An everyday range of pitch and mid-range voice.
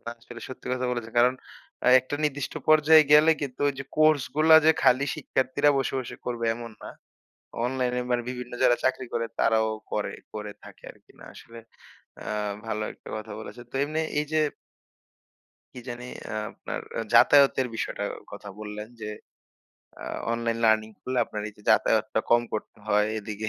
No: average, 3.4 semitones; low, 120 Hz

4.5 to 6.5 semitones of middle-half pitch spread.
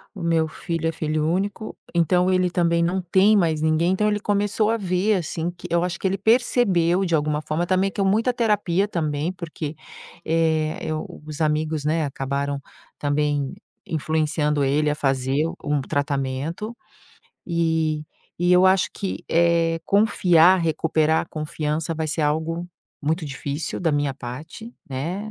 No: average, 3.3 semitones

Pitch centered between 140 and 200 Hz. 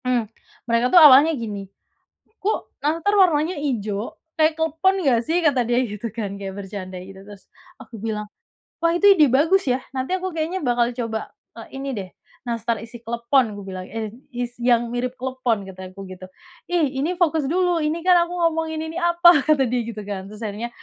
No: very high, 250 Hz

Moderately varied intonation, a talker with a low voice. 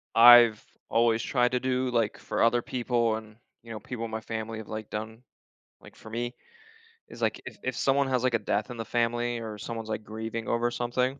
No: narrow, 1.6 semitones; low, 115 Hz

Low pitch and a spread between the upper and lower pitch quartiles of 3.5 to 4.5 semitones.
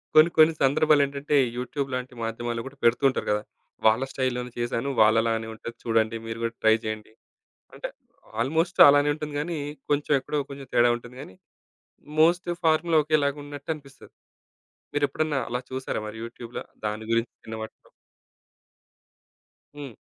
Yes: low, 130 Hz; average, 4.1 semitones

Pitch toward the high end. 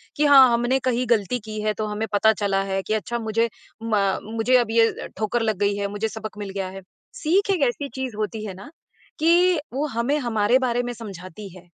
Yes: high, 225 Hz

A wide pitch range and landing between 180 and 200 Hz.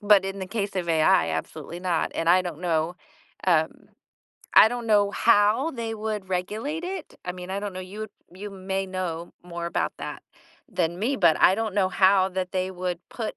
No: average, 2.8 semitones; high, 190 Hz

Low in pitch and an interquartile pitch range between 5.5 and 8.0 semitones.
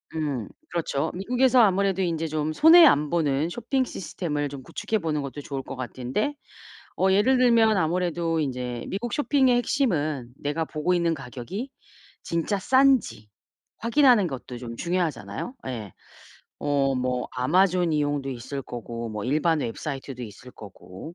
No: medium, 155 Hz; wide, 6.9 semitones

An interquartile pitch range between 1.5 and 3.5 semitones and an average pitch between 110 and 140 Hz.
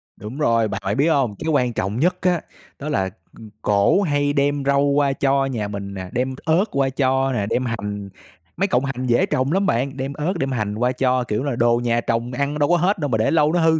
No: average, 3.9 semitones; low, 135 Hz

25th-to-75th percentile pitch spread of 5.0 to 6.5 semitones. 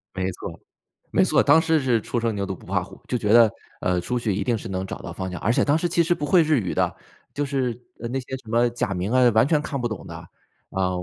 Yes: wide, 5.6 semitones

